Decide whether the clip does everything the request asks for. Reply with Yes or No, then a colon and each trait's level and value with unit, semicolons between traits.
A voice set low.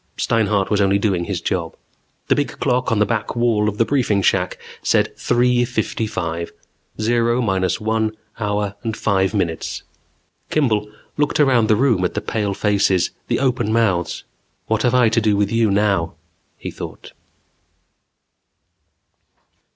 Yes: low, 110 Hz